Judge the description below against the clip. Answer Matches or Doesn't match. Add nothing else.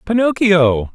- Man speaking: Matches